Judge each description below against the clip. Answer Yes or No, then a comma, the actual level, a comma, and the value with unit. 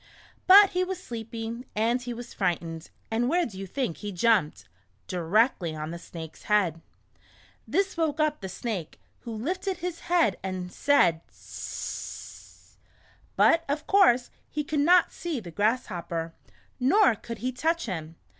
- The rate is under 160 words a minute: Yes, average, 150 wpm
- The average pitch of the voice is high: Yes, high, 230 Hz